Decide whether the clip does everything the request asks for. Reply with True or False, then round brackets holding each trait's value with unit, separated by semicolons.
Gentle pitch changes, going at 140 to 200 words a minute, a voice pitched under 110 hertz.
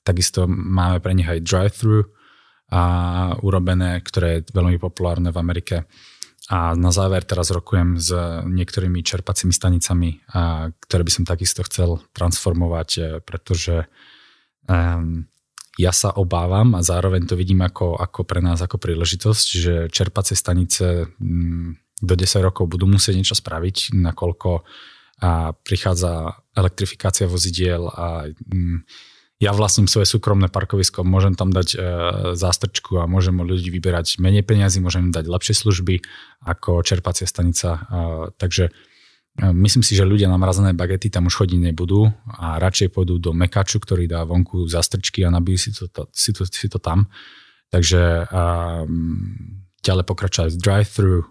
True (2.0 semitones; 145 wpm; 90 Hz)